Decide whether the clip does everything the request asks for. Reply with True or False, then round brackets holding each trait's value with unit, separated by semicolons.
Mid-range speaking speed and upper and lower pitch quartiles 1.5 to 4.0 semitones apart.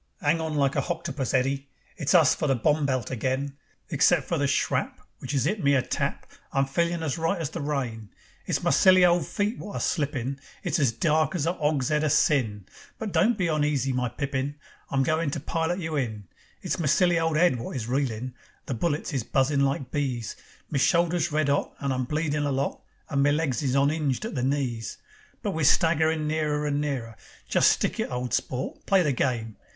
False (210 wpm; 3.5 semitones)